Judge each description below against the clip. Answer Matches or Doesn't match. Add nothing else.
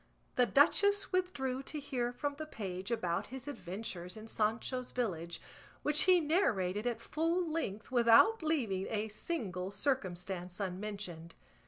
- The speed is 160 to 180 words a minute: Doesn't match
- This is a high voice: Matches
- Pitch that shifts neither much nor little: Doesn't match